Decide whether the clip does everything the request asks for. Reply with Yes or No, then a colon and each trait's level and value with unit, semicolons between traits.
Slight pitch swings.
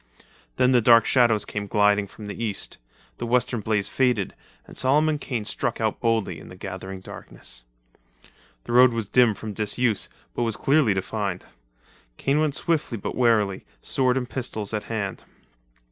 No: average, 3.5 semitones